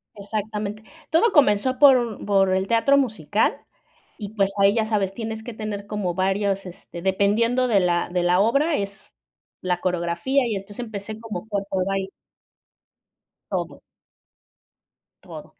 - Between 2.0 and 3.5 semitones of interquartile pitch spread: Yes, average, 2.8 semitones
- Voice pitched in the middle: No, high, 205 Hz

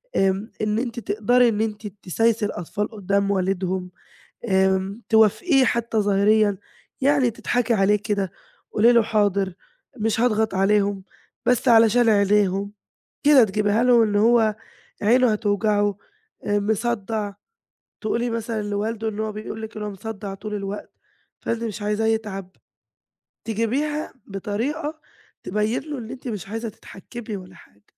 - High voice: Yes, high, 215 Hz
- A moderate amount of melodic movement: No, narrow, 2.2 semitones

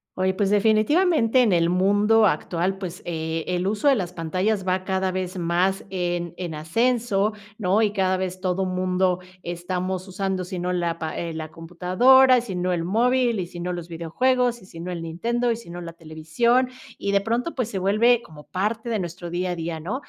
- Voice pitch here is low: No, medium, 185 Hz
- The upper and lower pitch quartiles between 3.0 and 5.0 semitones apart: Yes, average, 3.9 semitones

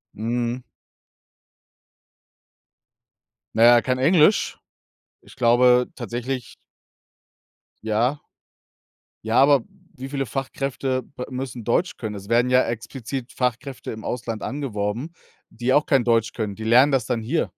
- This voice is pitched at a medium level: No, low, 125 Hz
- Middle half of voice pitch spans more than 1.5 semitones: Yes, average, 2.7 semitones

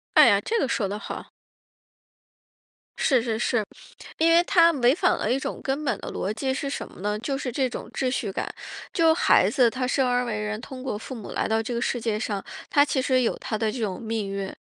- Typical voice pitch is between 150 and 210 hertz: No, high, 245 Hz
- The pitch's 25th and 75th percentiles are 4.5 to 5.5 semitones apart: No, average, 3.7 semitones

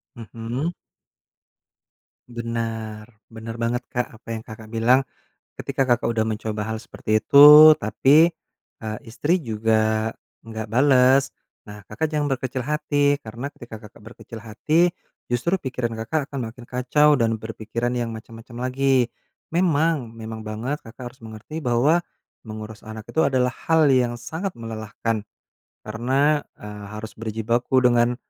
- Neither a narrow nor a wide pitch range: Yes, average, 3.6 semitones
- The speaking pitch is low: Yes, low, 120 Hz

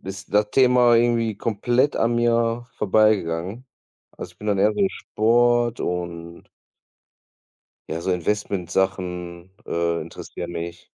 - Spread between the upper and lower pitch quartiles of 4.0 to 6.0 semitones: Yes, average, 5.2 semitones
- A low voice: Yes, low, 105 Hz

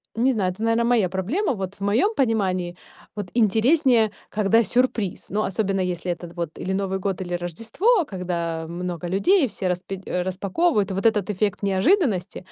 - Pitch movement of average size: Yes, average, 3.9 semitones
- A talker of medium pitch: No, high, 195 Hz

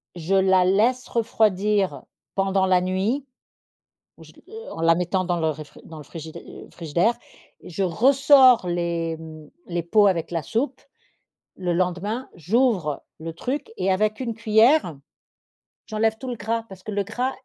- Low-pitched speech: No, high, 190 Hz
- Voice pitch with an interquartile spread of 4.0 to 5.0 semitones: Yes, average, 4.7 semitones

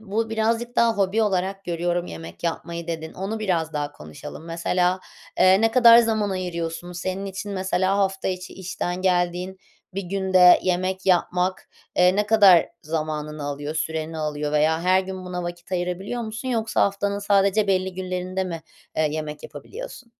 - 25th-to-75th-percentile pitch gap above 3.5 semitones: No, average, 2.8 semitones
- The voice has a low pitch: No, medium, 185 Hz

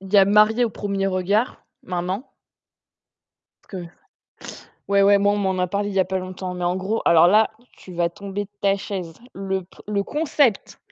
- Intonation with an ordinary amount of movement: No, narrow, 1.8 semitones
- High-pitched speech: Yes, high, 195 Hz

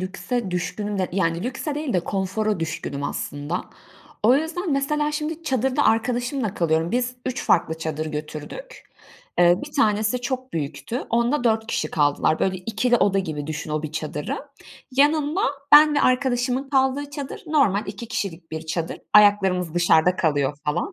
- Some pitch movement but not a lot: No, wide, 8.0 semitones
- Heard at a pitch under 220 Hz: Yes, high, 210 Hz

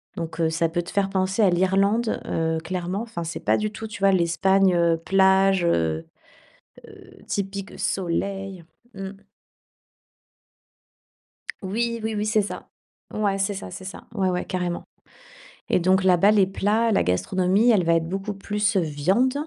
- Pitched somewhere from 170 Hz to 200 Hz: Yes, high, 190 Hz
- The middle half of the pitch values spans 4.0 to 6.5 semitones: No, average, 2.8 semitones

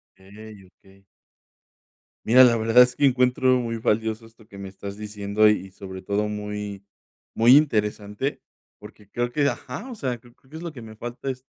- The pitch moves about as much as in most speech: Yes, average, 3.4 semitones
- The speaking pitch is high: No, low, 110 Hz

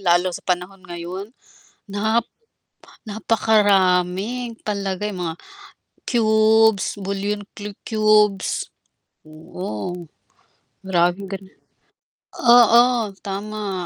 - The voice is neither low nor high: No, high, 200 Hz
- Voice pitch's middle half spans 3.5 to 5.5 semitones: No, average, 2.9 semitones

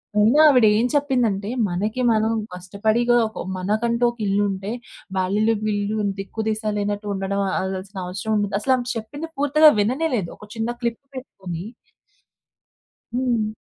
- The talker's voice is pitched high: Yes, high, 215 Hz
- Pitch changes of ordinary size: Yes, average, 3.2 semitones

